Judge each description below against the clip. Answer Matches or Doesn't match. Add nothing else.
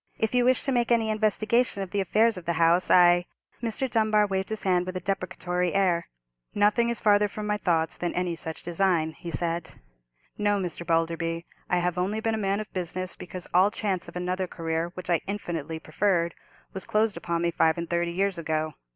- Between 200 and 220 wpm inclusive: Matches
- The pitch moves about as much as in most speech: Matches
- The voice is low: Doesn't match